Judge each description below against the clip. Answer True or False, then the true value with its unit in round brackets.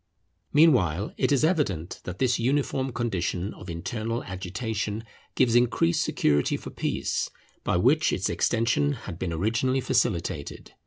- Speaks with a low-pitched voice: True (110 Hz)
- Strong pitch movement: True (6.2 semitones)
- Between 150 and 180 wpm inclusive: False (135 wpm)